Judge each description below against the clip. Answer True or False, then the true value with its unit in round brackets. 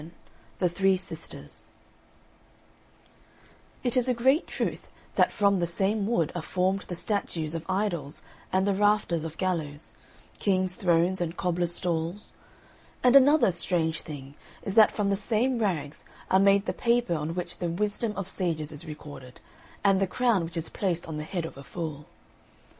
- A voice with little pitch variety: False (3.6 semitones)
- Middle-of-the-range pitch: True (180 Hz)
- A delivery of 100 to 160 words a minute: False (170 wpm)